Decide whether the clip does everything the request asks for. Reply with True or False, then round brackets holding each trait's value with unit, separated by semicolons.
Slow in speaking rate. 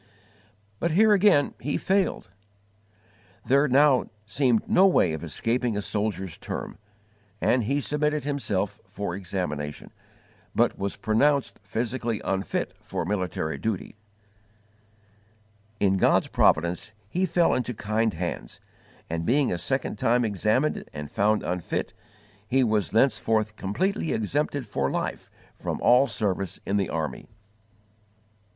True (125 wpm)